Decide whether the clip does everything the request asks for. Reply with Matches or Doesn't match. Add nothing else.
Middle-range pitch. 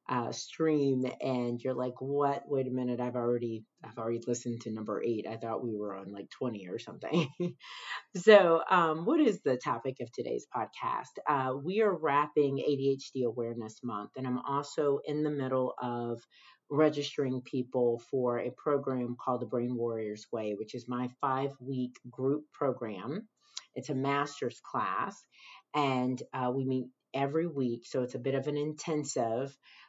Doesn't match